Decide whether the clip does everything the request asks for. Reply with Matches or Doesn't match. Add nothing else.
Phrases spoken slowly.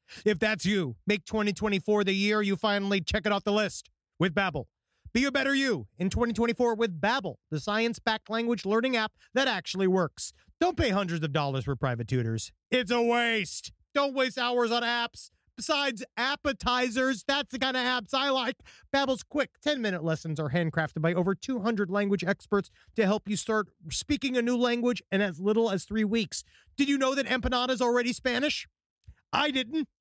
Doesn't match